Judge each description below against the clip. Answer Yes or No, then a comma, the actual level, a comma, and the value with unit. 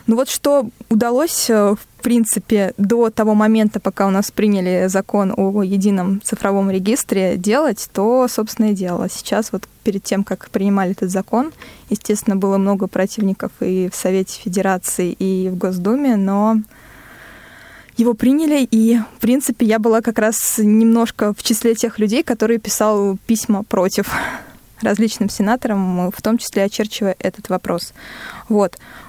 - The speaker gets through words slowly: No, average, 145 wpm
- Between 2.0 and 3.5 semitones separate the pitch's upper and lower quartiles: Yes, average, 2.9 semitones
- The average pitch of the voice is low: No, high, 210 Hz